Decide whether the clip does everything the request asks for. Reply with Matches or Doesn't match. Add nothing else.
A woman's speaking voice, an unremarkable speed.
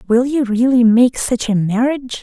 Matches